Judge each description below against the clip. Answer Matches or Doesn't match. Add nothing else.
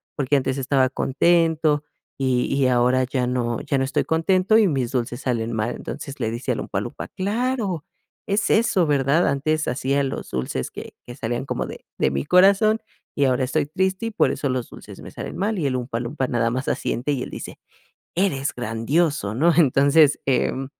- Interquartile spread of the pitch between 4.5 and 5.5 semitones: Matches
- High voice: Doesn't match